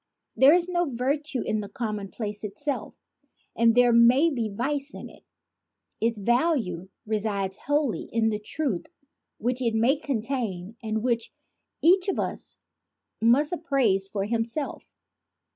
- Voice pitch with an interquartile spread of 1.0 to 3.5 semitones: No, average, 4.8 semitones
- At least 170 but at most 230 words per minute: No, slow, 135 wpm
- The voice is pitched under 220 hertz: No, high, 235 Hz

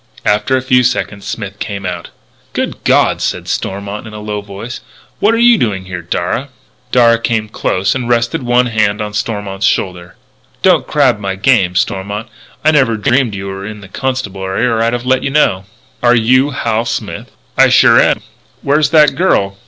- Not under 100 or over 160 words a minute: No, average, 185 wpm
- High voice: No, low, 110 Hz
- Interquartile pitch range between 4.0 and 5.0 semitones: Yes, average, 4.3 semitones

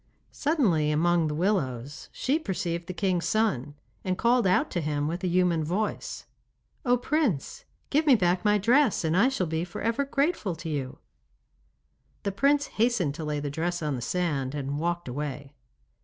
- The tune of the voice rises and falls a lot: Yes, wide, 6.7 semitones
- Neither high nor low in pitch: Yes, medium, 175 Hz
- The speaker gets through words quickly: No, average, 175 wpm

